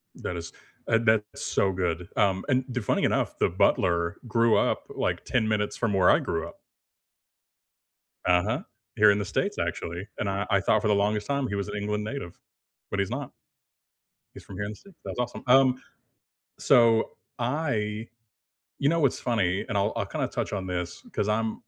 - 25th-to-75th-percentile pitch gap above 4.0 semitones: No, average, 3.1 semitones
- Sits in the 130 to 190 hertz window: No, low, 105 Hz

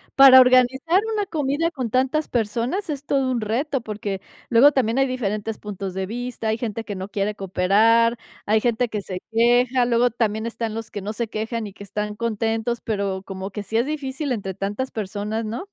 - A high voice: Yes, high, 230 Hz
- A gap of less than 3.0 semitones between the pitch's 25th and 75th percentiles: No, average, 3.4 semitones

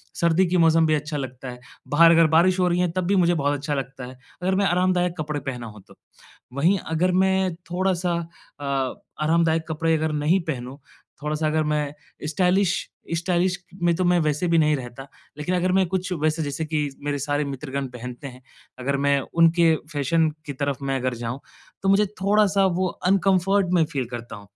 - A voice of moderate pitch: Yes, medium, 160 Hz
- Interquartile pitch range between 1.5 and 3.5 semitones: No, average, 4.2 semitones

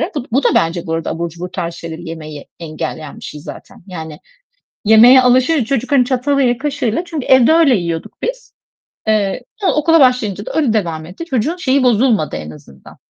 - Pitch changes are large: Yes, wide, 8.3 semitones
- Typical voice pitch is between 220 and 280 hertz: Yes, high, 225 Hz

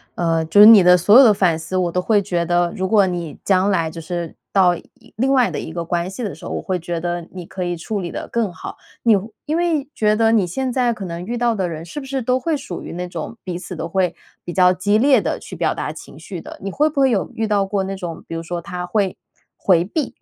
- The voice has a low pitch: No, high, 190 Hz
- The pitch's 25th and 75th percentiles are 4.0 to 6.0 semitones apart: Yes, average, 4.4 semitones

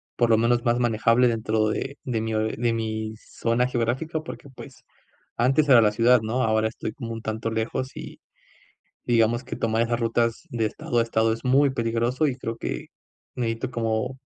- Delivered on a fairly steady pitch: Yes, narrow, 1.7 semitones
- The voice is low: Yes, low, 115 Hz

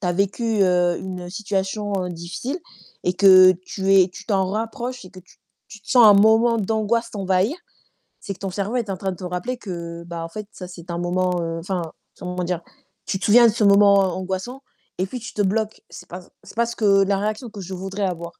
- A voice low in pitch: No, high, 195 Hz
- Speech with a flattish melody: No, average, 3.0 semitones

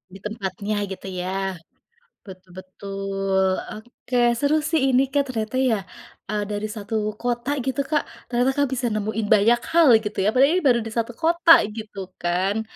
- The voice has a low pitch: No, high, 220 Hz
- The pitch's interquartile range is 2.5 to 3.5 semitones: No, average, 4.2 semitones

